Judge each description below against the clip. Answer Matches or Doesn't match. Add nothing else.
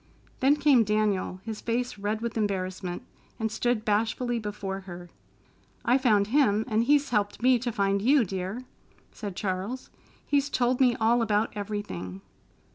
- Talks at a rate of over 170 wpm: Doesn't match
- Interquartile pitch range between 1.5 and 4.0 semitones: Matches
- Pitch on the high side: Matches